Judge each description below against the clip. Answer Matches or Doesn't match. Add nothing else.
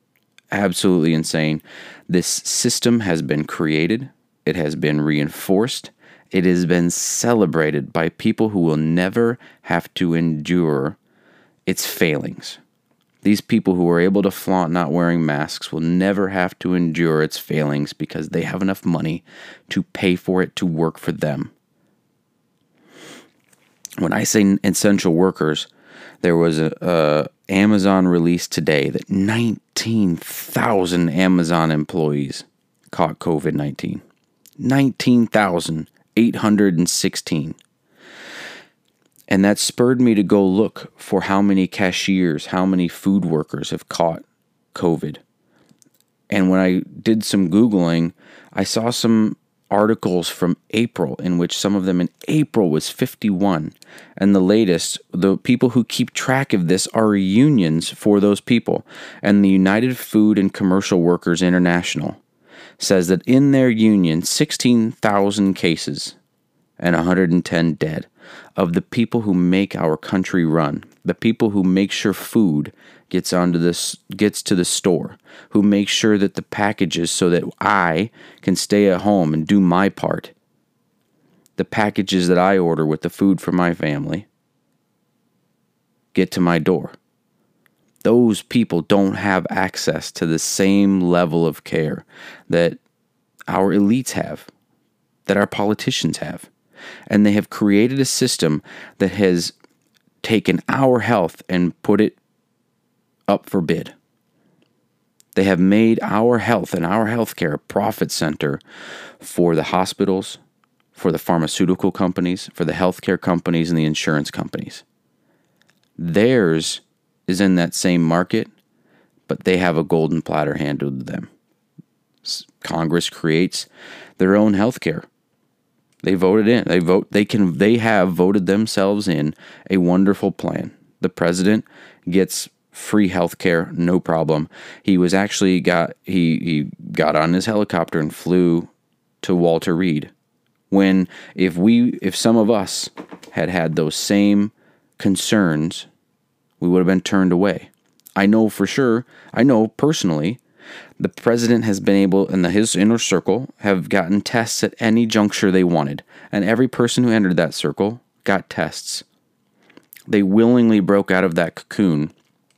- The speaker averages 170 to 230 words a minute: Doesn't match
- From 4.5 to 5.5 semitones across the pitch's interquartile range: Doesn't match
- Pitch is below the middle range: Matches